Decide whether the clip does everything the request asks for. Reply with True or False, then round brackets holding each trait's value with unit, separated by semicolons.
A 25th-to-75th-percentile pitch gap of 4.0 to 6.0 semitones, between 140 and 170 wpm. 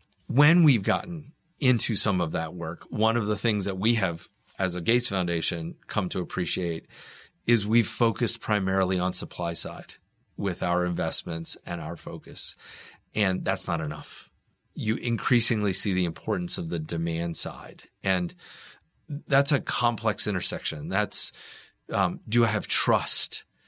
True (4.6 semitones; 150 wpm)